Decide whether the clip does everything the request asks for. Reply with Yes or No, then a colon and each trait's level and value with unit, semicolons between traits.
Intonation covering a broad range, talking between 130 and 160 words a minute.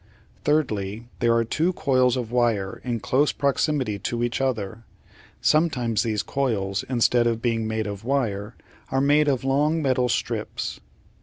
No: average, 3.6 semitones; average, 150 wpm